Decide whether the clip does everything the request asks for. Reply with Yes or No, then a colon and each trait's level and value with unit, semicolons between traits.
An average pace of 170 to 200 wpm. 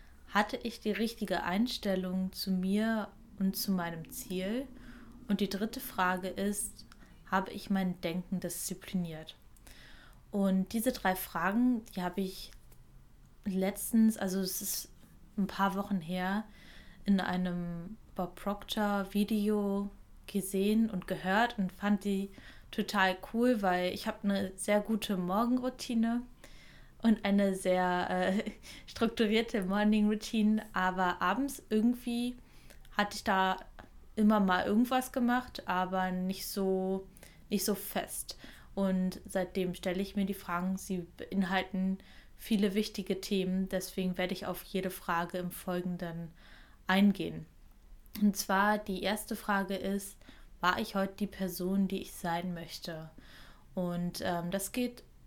No: average, 130 wpm